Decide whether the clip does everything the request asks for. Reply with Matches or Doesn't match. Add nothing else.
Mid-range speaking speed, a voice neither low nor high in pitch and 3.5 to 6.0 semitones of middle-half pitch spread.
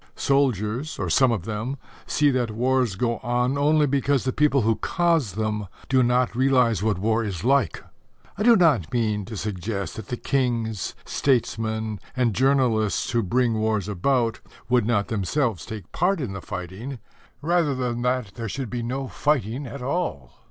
Doesn't match